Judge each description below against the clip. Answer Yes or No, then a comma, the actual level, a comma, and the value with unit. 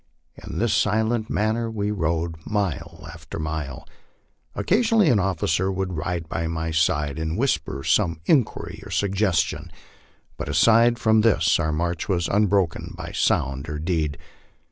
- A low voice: Yes, very low, 90 Hz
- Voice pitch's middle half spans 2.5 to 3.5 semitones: No, average, 5.2 semitones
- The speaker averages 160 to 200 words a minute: No, average, 150 wpm